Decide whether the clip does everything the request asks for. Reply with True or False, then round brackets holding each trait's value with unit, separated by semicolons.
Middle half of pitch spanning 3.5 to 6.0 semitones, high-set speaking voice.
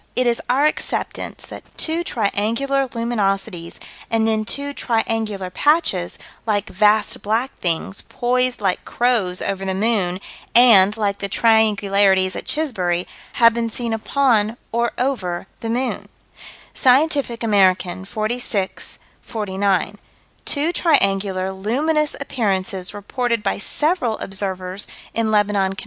True (4.1 semitones; 215 Hz)